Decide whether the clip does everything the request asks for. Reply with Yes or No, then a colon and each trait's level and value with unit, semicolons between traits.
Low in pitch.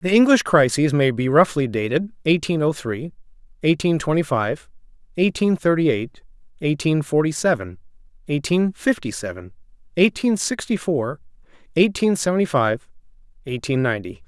No: medium, 150 Hz